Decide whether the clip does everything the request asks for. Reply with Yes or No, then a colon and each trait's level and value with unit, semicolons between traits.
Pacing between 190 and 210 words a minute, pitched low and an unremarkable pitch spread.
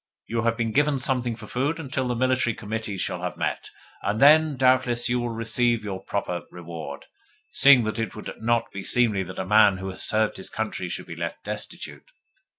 Yes: average, 200 wpm; low, 115 Hz; average, 3.6 semitones